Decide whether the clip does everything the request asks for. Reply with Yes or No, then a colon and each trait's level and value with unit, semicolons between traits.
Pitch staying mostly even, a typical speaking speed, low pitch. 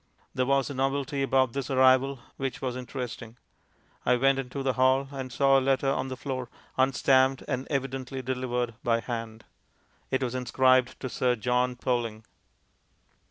Yes: narrow, 1.4 semitones; average, 160 wpm; low, 130 Hz